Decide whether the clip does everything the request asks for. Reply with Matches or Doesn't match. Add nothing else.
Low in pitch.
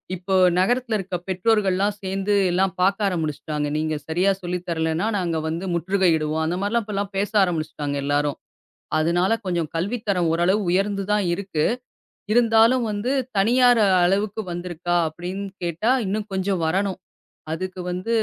Doesn't match